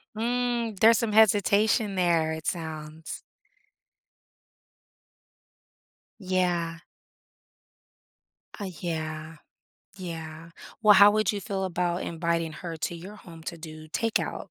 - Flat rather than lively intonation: No, average, 4.2 semitones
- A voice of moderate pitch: Yes, medium, 175 Hz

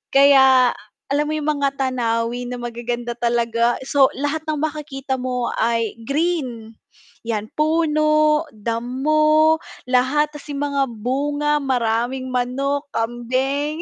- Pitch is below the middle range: No, very high, 265 Hz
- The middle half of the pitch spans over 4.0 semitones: No, average, 3.7 semitones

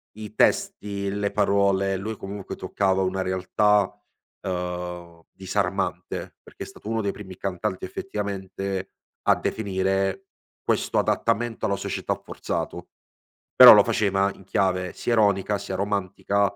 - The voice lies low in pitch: Yes, low, 100 Hz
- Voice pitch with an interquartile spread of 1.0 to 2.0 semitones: Yes, narrow, 1.5 semitones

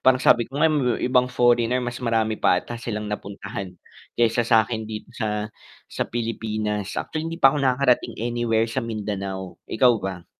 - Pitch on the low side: Yes, low, 115 Hz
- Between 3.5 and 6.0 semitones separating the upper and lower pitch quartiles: No, average, 2.8 semitones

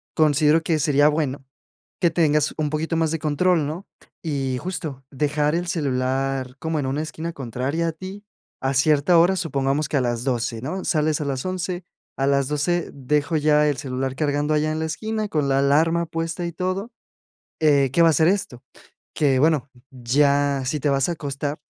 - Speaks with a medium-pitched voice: Yes, medium, 150 Hz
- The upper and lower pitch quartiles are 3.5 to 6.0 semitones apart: No, average, 3.1 semitones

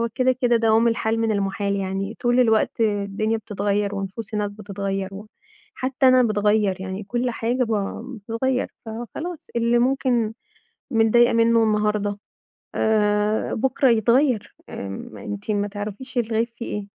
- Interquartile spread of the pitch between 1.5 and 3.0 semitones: Yes, average, 2.7 semitones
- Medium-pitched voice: No, high, 220 Hz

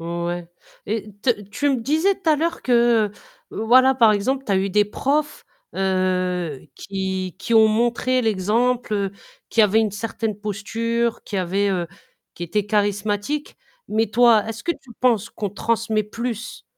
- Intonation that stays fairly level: No, average, 3.3 semitones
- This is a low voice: No, high, 215 Hz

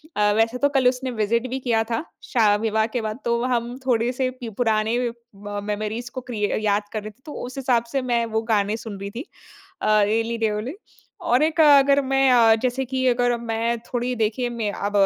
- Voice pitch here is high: Yes, high, 235 Hz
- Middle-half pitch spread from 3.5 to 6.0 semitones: No, average, 2.7 semitones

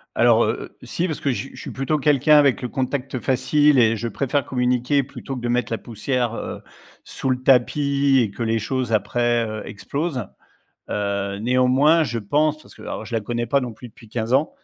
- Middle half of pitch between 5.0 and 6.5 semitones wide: No, average, 3.3 semitones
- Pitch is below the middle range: Yes, low, 125 Hz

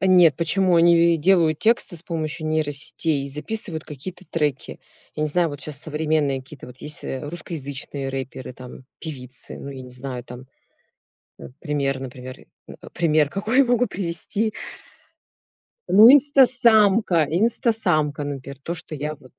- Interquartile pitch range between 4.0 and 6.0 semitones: Yes, average, 4.7 semitones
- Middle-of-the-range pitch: Yes, medium, 155 Hz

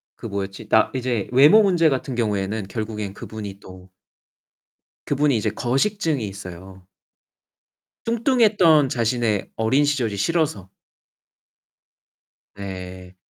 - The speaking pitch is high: No, low, 115 Hz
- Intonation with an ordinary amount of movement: No, wide, 6.8 semitones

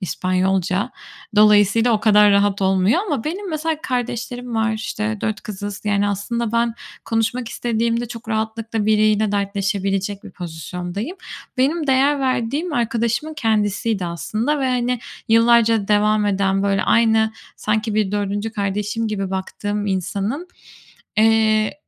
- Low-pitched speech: No, high, 215 Hz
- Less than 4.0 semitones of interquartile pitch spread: Yes, average, 2.8 semitones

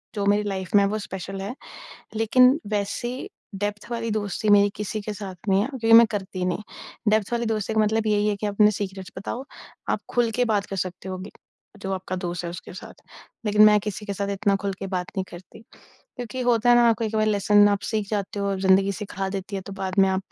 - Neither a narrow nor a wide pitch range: No, narrow, 1.9 semitones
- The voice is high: Yes, high, 205 Hz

